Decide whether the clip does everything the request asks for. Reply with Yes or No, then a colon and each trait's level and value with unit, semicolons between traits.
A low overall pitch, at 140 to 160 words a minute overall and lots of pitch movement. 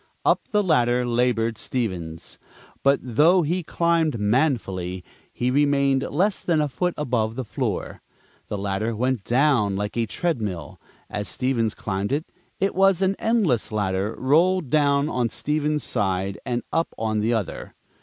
Yes: low, 125 Hz; average, 145 wpm; wide, 6.1 semitones